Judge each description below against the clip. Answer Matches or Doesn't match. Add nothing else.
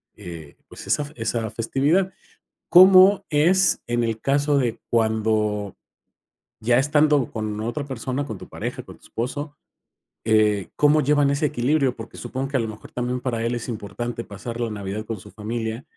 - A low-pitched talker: Matches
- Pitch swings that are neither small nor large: Matches